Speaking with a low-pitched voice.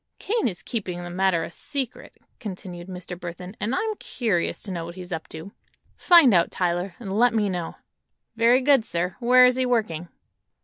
No: high, 190 Hz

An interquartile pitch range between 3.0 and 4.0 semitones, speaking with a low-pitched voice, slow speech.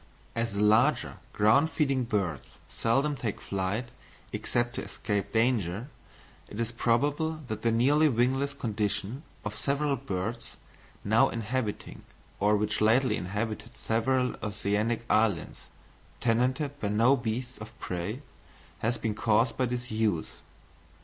Yes: average, 3.5 semitones; low, 115 Hz; slow, 125 wpm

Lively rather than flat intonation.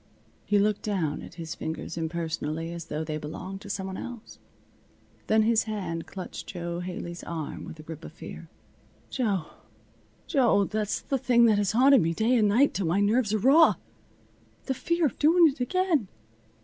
Yes: wide, 6.3 semitones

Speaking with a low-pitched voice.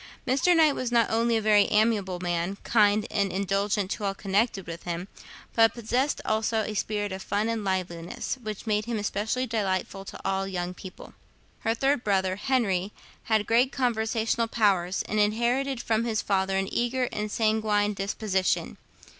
No: high, 210 Hz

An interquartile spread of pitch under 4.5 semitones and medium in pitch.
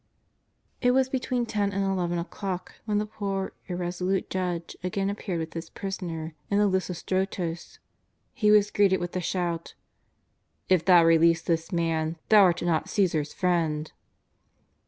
Yes: average, 2.9 semitones; medium, 180 Hz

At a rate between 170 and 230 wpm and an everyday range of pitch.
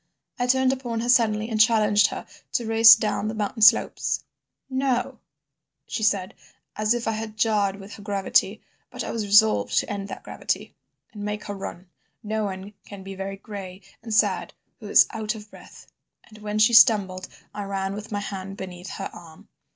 No: average, 180 wpm; narrow, 2.1 semitones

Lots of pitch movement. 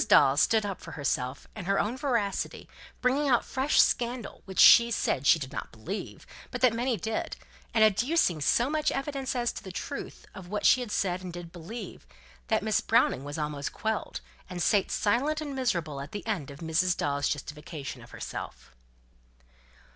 Yes: wide, 7.4 semitones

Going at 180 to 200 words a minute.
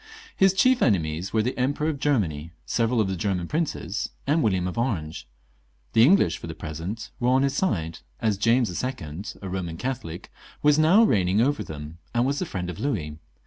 Yes: average, 190 wpm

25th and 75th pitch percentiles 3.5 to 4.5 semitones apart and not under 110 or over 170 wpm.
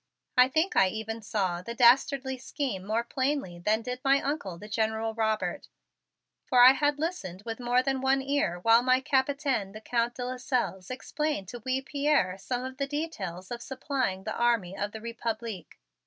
No: average, 3.9 semitones; average, 180 wpm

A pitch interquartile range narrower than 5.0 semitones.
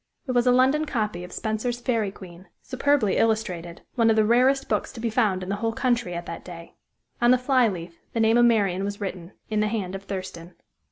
Yes: average, 4.5 semitones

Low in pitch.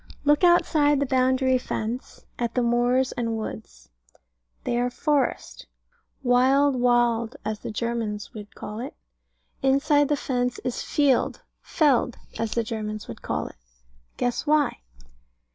No: high, 245 Hz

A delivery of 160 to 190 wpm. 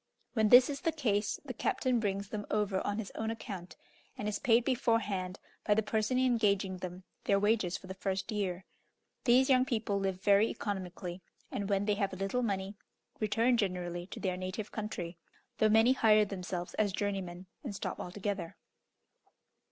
Yes: average, 175 wpm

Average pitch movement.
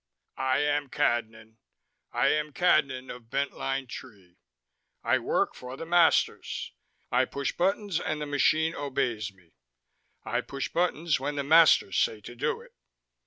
Yes: average, 4.2 semitones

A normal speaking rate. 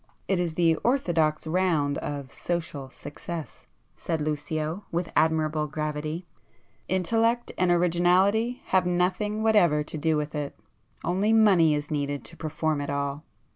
No: slow, 130 wpm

